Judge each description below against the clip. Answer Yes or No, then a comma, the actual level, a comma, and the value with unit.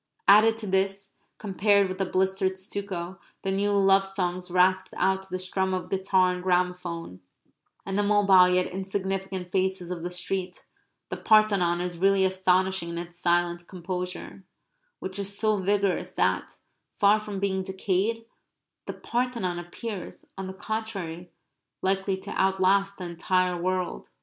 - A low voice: No, high, 190 Hz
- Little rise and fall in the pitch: Yes, narrow, 1.5 semitones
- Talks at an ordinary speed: Yes, average, 150 wpm